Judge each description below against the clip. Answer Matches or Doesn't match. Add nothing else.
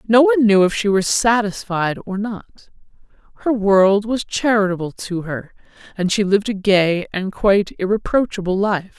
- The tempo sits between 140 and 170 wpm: Matches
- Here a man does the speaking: Doesn't match